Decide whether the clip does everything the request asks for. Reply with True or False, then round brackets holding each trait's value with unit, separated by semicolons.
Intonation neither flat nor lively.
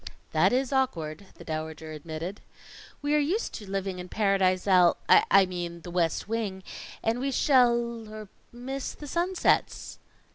False (6.2 semitones)